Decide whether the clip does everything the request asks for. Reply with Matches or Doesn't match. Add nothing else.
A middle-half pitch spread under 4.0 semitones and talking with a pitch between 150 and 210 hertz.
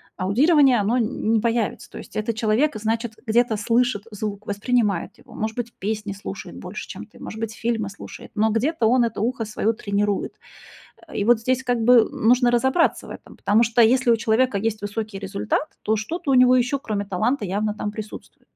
Doesn't match